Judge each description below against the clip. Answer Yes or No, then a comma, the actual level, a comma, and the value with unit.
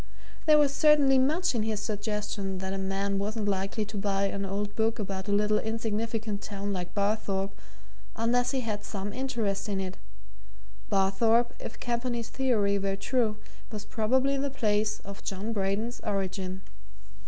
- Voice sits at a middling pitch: No, high, 210 Hz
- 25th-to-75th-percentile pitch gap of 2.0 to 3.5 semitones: Yes, average, 2.8 semitones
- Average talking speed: Yes, average, 155 wpm